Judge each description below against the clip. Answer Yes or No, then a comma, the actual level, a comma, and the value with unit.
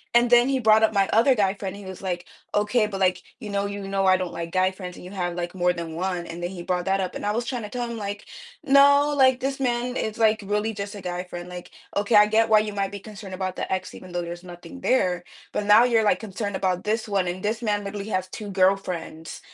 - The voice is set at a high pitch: Yes, high, 200 Hz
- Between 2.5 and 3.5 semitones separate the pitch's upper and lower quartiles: Yes, average, 3.2 semitones